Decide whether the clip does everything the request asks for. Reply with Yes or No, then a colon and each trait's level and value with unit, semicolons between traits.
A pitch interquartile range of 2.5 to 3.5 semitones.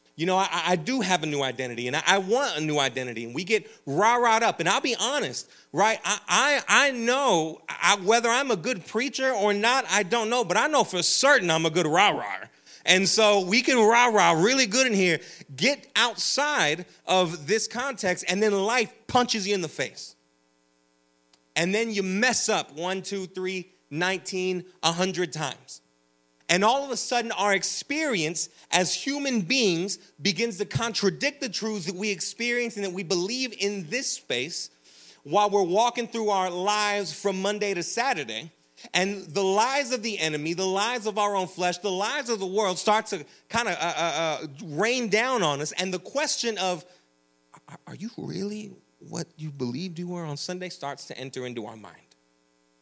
No: wide, 5.4 semitones